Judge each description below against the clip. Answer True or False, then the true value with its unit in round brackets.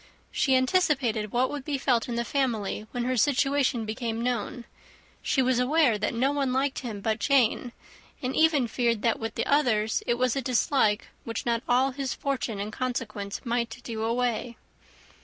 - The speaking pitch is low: False (245 Hz)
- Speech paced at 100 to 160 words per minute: False (175 wpm)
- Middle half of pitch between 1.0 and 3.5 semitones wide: True (2.9 semitones)